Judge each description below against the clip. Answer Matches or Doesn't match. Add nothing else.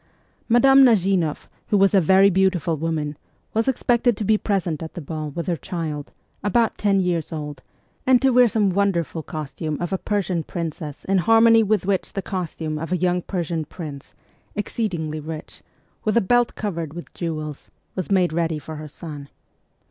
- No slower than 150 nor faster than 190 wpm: Matches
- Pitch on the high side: Doesn't match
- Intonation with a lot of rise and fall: Doesn't match